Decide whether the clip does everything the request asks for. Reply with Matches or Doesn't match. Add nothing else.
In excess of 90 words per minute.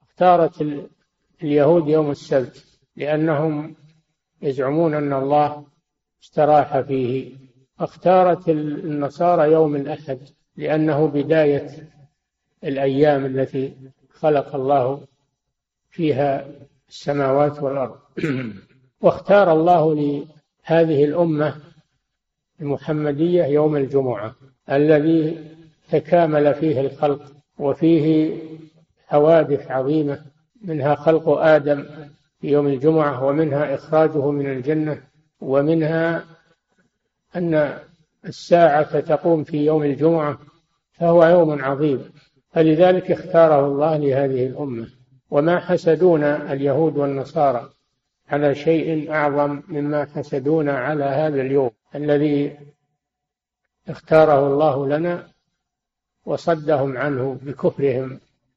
Doesn't match